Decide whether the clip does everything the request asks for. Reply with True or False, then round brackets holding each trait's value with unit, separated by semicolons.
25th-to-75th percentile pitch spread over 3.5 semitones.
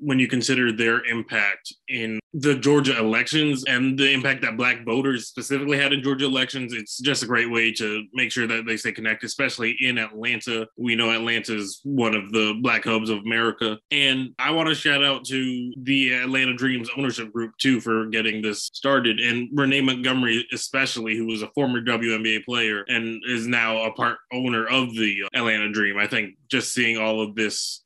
False (2.9 semitones)